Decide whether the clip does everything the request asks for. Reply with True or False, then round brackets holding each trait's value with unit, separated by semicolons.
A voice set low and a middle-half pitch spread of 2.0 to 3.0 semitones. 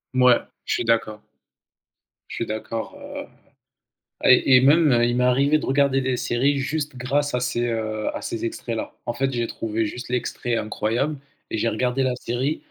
True (125 Hz; 2.7 semitones)